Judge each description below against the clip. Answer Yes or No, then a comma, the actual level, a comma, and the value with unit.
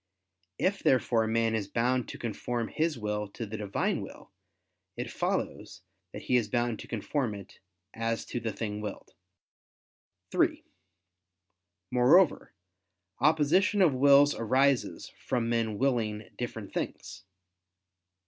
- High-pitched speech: No, low, 115 Hz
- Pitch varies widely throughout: No, average, 3.8 semitones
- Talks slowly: Yes, slow, 125 wpm